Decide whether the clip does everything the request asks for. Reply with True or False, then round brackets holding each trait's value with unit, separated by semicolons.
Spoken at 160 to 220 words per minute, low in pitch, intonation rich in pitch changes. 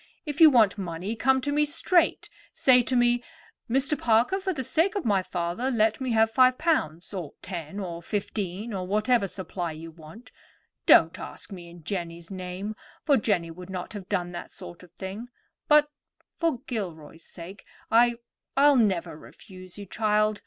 False (170 wpm; 205 Hz; 5.8 semitones)